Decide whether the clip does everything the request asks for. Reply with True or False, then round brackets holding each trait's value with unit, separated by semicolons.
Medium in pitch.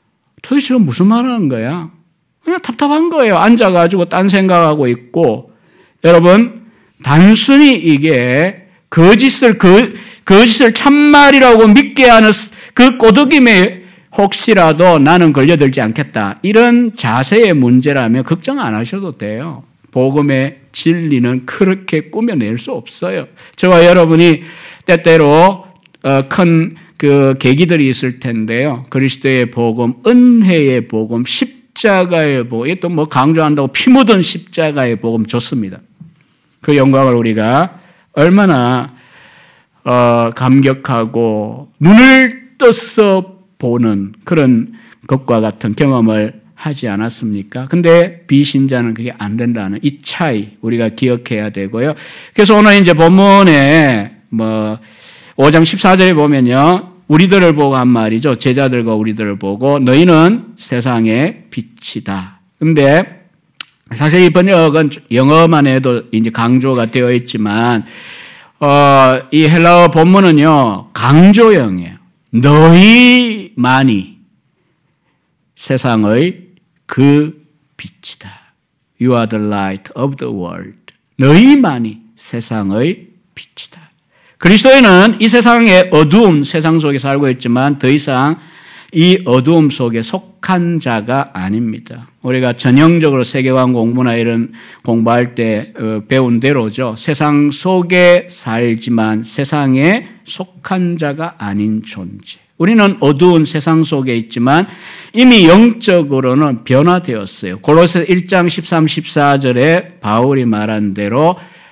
True (150 Hz)